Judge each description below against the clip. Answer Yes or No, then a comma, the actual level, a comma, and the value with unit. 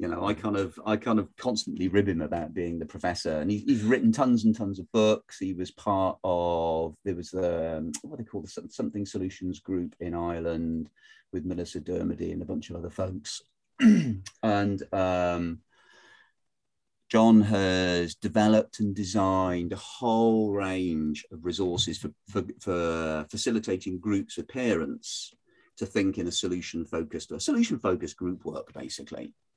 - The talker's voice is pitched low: Yes, very low, 95 Hz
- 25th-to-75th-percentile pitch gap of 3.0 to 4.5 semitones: Yes, average, 3.5 semitones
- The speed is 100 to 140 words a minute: No, average, 160 wpm